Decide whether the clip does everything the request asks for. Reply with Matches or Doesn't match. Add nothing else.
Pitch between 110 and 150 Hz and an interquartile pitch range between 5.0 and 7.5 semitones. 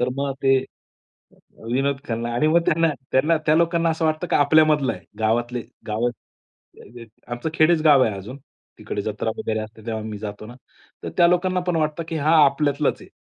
Matches